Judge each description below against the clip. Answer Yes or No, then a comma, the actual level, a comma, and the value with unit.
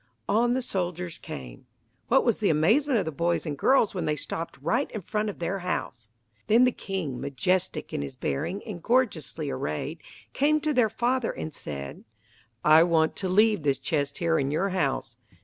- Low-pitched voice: No, medium, 180 Hz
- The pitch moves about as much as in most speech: No, wide, 6.8 semitones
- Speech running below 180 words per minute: No, average, 185 wpm